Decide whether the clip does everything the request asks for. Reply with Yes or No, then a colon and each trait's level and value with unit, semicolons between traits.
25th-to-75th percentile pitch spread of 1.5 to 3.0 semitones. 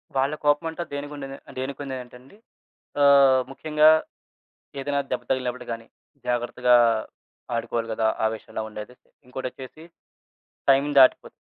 Yes: narrow, 2.4 semitones